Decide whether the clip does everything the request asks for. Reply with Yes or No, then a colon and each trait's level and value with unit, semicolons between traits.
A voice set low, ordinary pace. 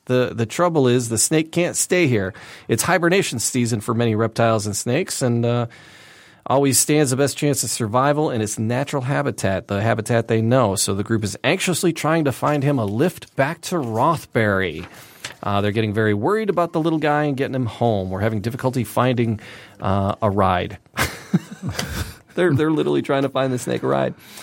Yes: low, 120 Hz; average, 190 wpm